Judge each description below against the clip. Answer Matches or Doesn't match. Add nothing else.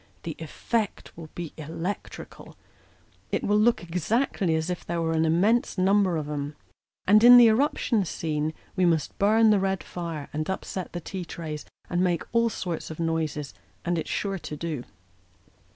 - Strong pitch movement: Doesn't match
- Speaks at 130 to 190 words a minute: Matches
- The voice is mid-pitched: Matches